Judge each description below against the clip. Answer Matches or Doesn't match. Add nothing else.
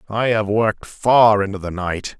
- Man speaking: Matches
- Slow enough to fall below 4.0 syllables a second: Doesn't match